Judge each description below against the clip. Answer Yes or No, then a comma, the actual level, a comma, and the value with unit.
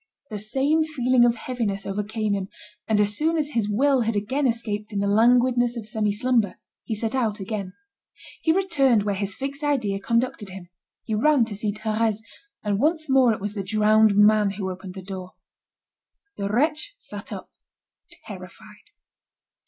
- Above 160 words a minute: Yes, average, 170 wpm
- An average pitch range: Yes, average, 3.9 semitones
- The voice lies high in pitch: Yes, high, 220 Hz